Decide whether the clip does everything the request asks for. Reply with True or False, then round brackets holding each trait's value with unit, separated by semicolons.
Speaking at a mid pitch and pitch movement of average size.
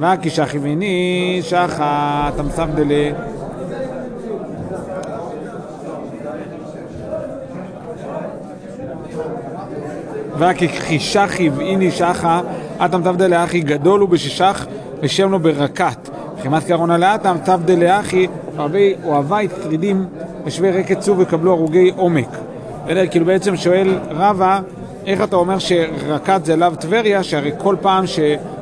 True (175 Hz; 3.1 semitones)